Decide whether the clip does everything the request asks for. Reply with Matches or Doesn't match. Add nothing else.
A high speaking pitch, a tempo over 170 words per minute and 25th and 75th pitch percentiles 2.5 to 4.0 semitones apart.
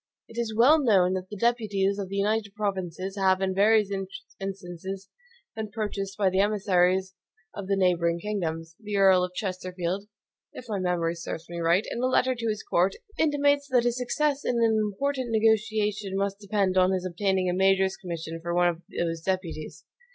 Matches